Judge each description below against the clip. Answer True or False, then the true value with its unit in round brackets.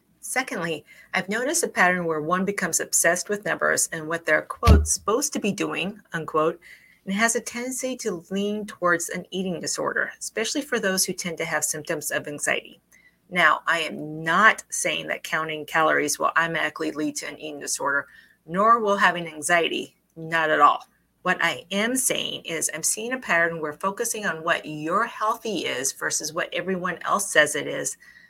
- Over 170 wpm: True (180 wpm)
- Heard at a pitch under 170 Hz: False (180 Hz)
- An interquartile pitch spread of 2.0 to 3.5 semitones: False (4.9 semitones)